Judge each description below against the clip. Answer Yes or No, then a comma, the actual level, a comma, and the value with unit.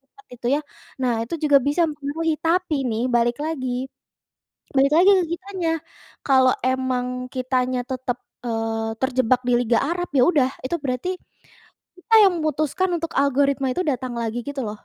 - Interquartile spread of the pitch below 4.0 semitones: No, average, 4.5 semitones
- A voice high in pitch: Yes, very high, 270 Hz